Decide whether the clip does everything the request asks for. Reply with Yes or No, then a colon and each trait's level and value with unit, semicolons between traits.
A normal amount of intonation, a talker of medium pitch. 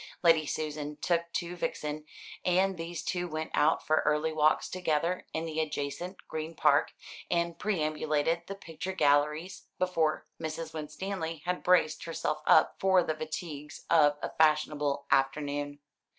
No: narrow, 2.2 semitones; medium, 155 Hz